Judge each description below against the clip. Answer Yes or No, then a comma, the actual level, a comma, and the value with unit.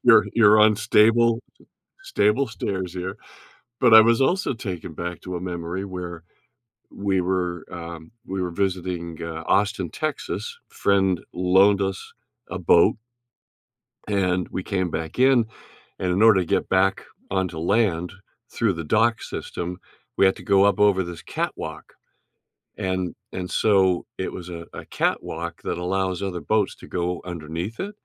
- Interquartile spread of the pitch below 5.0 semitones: Yes, average, 2.8 semitones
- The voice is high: No, very low, 95 Hz